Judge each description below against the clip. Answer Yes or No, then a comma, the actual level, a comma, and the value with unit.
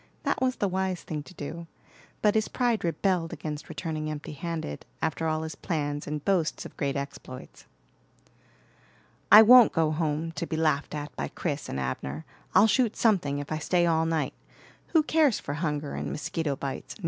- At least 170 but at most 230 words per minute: Yes, average, 180 wpm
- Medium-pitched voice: Yes, medium, 160 Hz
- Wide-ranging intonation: No, average, 4.0 semitones